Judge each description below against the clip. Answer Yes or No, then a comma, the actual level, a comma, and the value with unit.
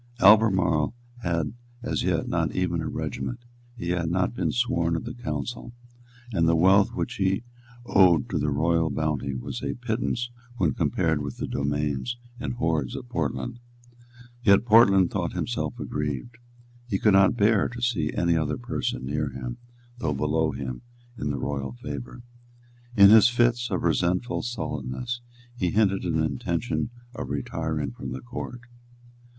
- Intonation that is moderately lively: No, wide, 7.1 semitones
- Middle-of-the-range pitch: No, very low, 85 Hz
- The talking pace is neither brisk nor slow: Yes, average, 155 wpm